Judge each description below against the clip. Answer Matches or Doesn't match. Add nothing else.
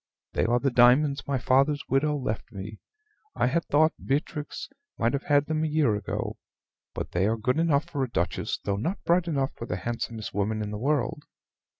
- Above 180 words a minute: Matches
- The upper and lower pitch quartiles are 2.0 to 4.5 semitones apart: Doesn't match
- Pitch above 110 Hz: Matches